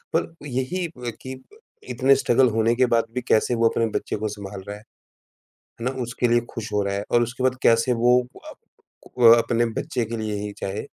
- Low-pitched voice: Yes, low, 120 Hz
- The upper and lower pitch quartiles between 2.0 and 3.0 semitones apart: Yes, narrow, 2.5 semitones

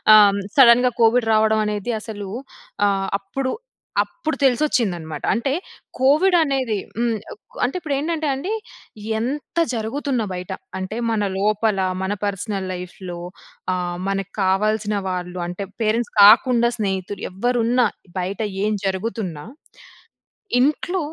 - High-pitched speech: Yes, high, 220 Hz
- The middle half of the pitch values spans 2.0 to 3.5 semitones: No, average, 4.7 semitones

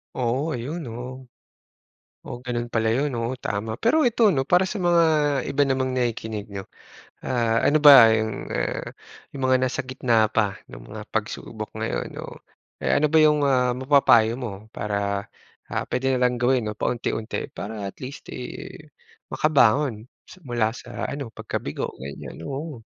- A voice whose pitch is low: Yes, low, 125 Hz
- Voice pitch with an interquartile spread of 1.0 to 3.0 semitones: No, average, 3.7 semitones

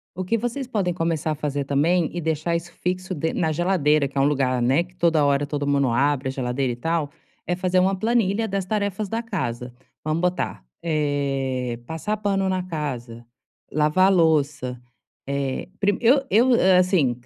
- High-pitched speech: No, medium, 160 Hz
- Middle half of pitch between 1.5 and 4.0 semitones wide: No, average, 4.9 semitones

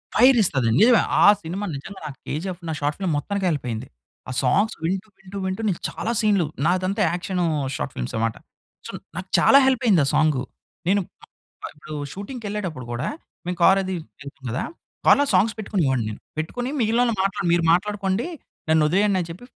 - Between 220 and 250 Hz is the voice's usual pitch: No, medium, 185 Hz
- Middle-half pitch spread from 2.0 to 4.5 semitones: No, average, 5.0 semitones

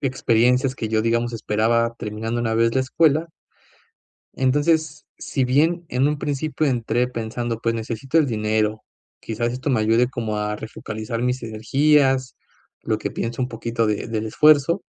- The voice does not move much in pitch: No, average, 3.2 semitones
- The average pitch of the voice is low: Yes, low, 120 Hz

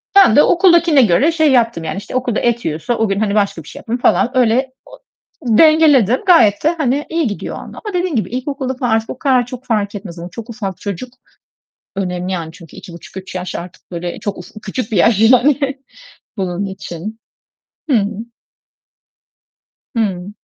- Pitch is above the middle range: Yes, high, 225 Hz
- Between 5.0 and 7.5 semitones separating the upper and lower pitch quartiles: Yes, average, 5.3 semitones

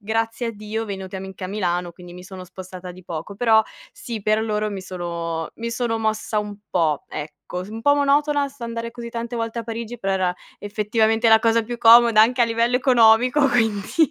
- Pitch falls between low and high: No, high, 220 Hz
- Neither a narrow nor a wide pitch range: Yes, average, 3.6 semitones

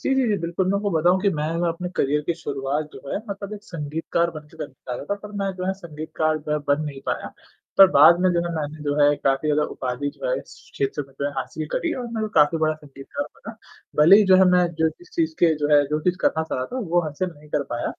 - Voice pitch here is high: No, medium, 160 Hz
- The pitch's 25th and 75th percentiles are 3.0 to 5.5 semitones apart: Yes, average, 4.4 semitones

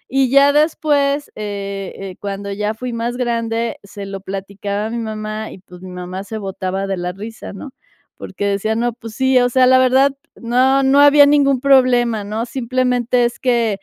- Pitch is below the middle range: No, high, 230 Hz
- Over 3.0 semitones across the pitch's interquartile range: Yes, average, 4.4 semitones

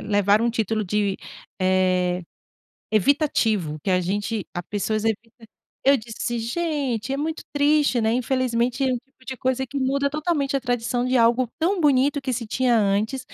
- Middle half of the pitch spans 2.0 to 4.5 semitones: Yes, average, 4.2 semitones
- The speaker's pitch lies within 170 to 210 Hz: No, high, 240 Hz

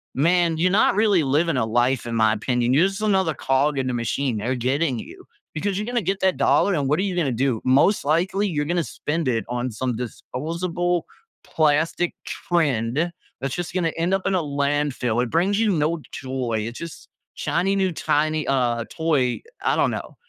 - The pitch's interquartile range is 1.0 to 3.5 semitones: No, wide, 5.6 semitones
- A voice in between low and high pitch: Yes, medium, 150 Hz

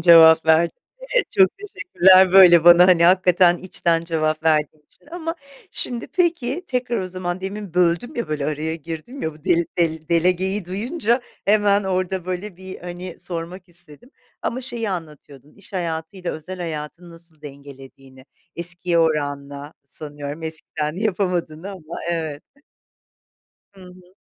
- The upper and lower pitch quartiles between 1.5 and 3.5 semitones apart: Yes, average, 3.1 semitones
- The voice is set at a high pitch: No, medium, 175 Hz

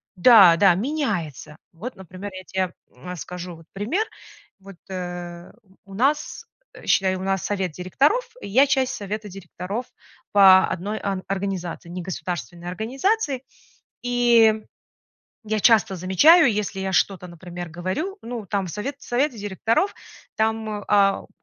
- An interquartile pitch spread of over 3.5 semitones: Yes, average, 4.2 semitones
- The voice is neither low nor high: No, high, 195 Hz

